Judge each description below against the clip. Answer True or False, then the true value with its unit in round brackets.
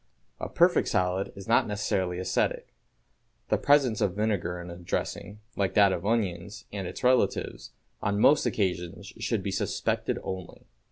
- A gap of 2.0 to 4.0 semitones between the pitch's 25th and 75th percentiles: True (3.0 semitones)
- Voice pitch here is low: True (100 Hz)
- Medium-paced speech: True (155 wpm)